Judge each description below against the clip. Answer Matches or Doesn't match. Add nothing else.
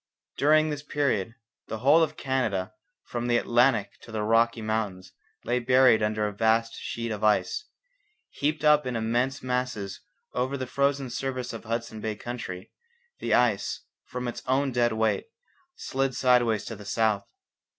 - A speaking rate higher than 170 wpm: Doesn't match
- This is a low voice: Matches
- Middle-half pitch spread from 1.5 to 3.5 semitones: Matches